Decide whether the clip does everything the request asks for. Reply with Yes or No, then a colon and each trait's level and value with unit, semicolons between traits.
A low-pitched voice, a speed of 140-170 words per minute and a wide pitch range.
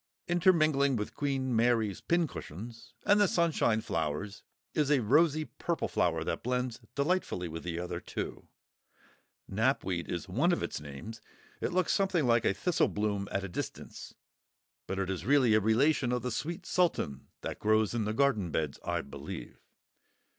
Yes: low, 120 Hz; average, 160 wpm; wide, 7.3 semitones